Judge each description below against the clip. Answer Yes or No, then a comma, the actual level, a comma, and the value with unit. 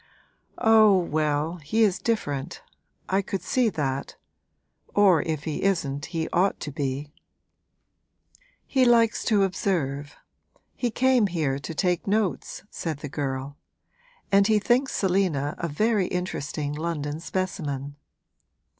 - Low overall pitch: No, medium, 170 Hz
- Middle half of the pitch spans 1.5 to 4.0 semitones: No, wide, 5.5 semitones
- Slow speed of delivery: Yes, slow, 125 wpm